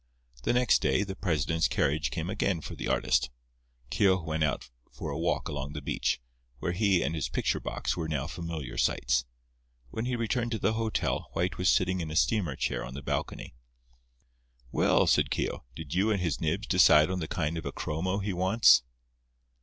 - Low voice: Yes, very low, 85 Hz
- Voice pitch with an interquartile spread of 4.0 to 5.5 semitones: Yes, average, 4.3 semitones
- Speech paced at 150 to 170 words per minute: No, average, 195 wpm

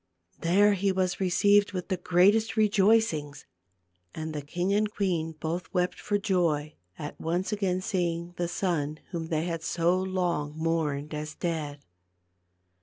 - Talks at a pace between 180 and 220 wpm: No, average, 145 wpm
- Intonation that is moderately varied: Yes, average, 3.4 semitones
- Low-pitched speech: No, medium, 175 Hz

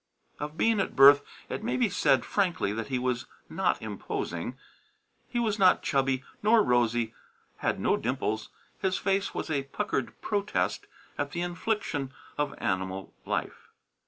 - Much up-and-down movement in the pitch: Yes, wide, 8.3 semitones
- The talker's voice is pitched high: No, medium, 140 Hz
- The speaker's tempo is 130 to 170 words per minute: Yes, average, 150 wpm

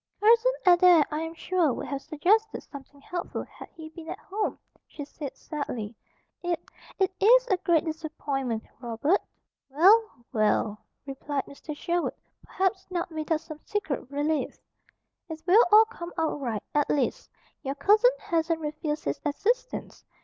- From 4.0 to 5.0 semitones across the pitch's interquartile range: Yes, average, 4.7 semitones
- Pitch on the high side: Yes, very high, 320 Hz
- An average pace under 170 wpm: Yes, average, 150 wpm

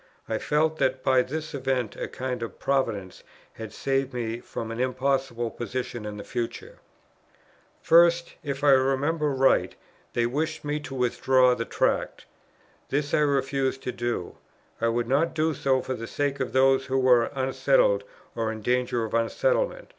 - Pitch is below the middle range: Yes, low, 130 Hz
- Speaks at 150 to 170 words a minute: Yes, average, 160 wpm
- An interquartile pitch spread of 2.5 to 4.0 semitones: Yes, average, 3.0 semitones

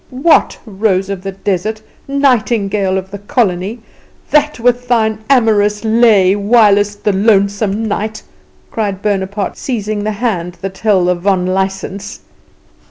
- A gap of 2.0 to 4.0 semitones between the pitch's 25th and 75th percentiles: Yes, narrow, 2.4 semitones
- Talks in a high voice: Yes, high, 205 Hz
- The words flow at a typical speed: No, slow, 125 wpm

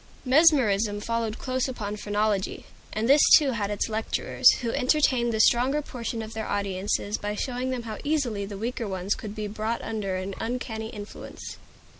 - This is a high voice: Yes, high, 220 Hz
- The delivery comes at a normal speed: Yes, average, 170 wpm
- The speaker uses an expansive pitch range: No, average, 3.3 semitones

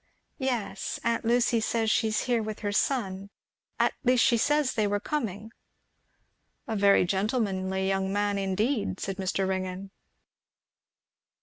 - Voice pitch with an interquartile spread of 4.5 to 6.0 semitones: No, average, 3.3 semitones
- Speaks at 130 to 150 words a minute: Yes, slow, 135 wpm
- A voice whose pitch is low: No, high, 205 Hz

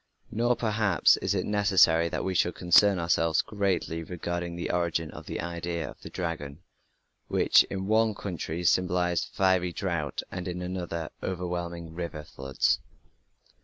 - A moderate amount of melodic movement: No, narrow, 2.1 semitones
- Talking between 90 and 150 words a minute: Yes, average, 145 wpm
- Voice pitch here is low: Yes, very low, 85 Hz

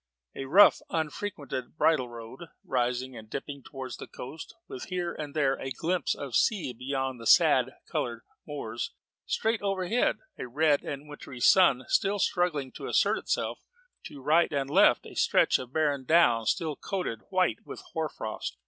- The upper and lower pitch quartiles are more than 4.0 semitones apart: Yes, average, 5.2 semitones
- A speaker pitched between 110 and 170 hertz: Yes, medium, 140 Hz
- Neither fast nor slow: Yes, average, 165 wpm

